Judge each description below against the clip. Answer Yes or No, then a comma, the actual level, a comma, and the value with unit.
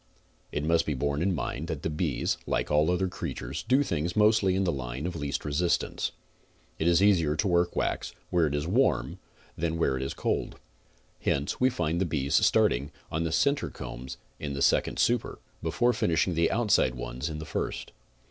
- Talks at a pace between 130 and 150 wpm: No, average, 195 wpm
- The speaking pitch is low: Yes, very low, 80 Hz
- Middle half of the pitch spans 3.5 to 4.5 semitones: Yes, average, 4.0 semitones